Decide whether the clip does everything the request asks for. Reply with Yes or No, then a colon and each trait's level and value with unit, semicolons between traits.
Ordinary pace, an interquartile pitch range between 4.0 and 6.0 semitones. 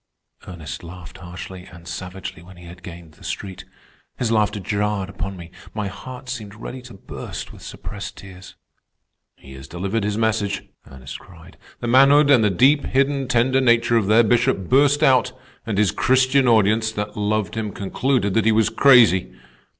Yes: average, 175 wpm; average, 4.7 semitones